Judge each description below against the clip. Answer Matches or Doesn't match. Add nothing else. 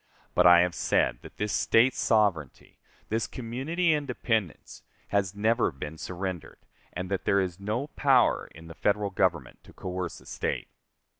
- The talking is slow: Doesn't match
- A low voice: Matches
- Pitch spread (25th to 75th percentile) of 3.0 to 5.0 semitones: Matches